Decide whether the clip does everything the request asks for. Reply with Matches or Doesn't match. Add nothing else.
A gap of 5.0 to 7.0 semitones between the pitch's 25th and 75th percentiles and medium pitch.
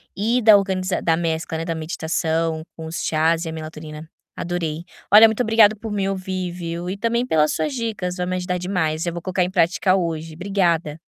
Doesn't match